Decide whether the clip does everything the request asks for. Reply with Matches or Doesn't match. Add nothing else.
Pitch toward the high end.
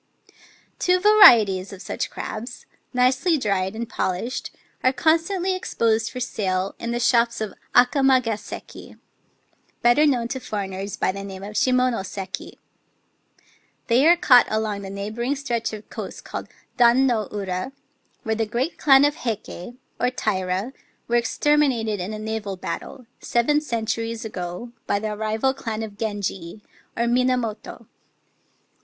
Matches